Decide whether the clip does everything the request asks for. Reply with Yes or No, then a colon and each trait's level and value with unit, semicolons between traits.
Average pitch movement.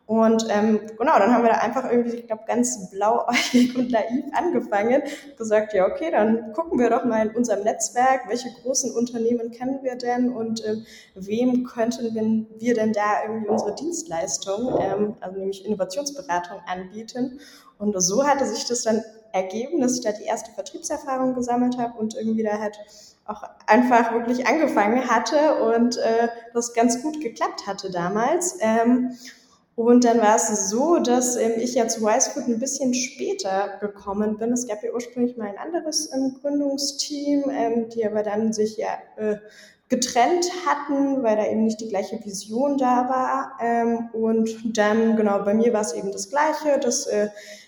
Yes: average, 3.1 semitones